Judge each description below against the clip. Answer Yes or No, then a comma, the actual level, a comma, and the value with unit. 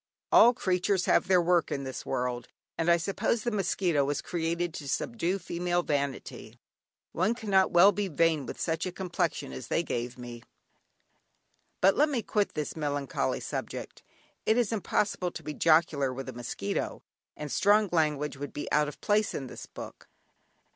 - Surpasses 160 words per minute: Yes, average, 170 wpm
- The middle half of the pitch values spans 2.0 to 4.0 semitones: No, average, 5.2 semitones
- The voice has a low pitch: No, medium, 170 Hz